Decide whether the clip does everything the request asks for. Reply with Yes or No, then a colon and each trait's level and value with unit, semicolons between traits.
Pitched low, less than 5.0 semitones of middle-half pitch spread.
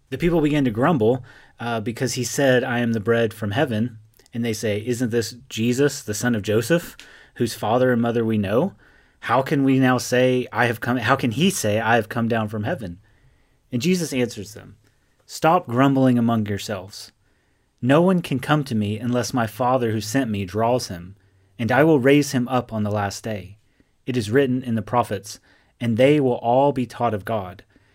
Yes: low, 120 Hz; average, 3.4 semitones